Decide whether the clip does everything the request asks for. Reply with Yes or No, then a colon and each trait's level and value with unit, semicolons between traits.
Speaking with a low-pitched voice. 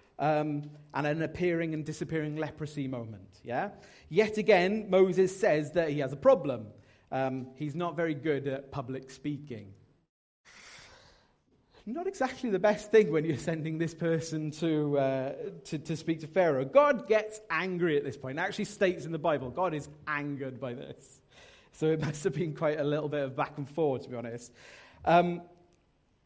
No: medium, 155 Hz